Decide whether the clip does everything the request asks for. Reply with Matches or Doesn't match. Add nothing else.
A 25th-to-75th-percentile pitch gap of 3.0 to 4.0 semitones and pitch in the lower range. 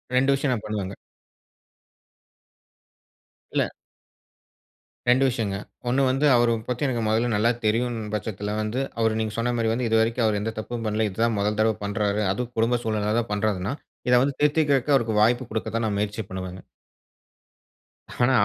Doesn't match